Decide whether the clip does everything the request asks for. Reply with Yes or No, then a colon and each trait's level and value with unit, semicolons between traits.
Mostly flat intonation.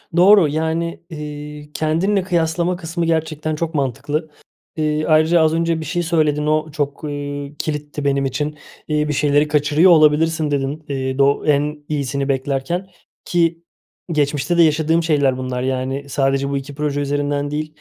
Yes: narrow, 2.2 semitones